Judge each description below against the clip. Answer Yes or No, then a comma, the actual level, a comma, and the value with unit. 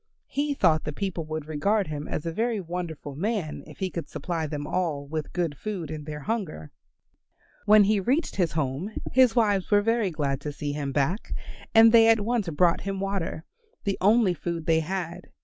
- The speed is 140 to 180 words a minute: No, average, 195 wpm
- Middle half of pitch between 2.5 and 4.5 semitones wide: No, average, 5.1 semitones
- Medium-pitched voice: Yes, medium, 175 Hz